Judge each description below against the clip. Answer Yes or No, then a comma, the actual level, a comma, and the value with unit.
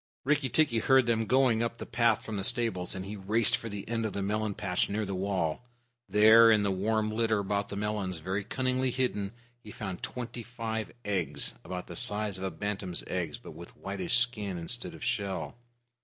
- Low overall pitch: Yes, low, 105 Hz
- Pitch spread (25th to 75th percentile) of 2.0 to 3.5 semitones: Yes, average, 3.1 semitones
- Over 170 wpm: Yes, average, 200 wpm